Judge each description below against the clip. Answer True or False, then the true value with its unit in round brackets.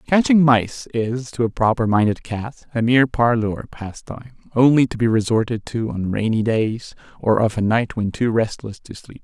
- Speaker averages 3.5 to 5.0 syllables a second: True (4.8 syllables/s)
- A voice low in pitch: True (115 Hz)